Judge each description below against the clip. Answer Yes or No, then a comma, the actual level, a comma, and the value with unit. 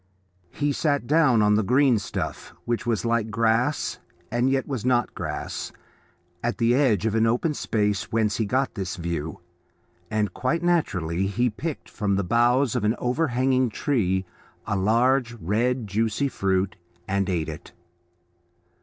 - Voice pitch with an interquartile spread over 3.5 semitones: Yes, average, 4.1 semitones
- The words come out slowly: No, average, 155 wpm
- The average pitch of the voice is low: Yes, low, 115 Hz